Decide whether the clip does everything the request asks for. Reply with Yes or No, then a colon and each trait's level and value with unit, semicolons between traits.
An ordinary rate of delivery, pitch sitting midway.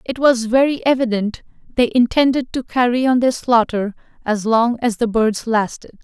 No: average, 170 wpm; high, 240 Hz